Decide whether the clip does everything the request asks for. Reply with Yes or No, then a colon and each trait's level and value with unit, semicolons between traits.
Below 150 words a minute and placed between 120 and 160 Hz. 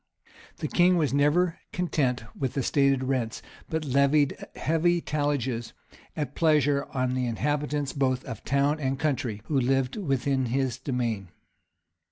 Yes: average, 140 wpm; medium, 140 Hz